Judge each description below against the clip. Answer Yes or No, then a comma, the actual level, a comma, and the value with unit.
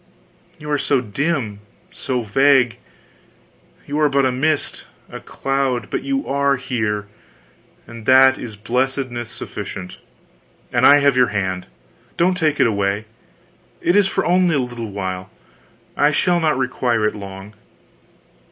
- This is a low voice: Yes, low, 130 Hz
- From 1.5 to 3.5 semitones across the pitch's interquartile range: No, average, 5.1 semitones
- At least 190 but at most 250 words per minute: No, average, 145 wpm